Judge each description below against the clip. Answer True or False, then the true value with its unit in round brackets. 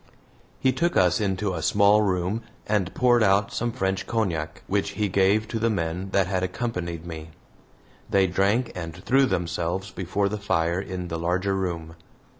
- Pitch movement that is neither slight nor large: True (3.1 semitones)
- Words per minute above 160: True (170 wpm)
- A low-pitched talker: True (95 Hz)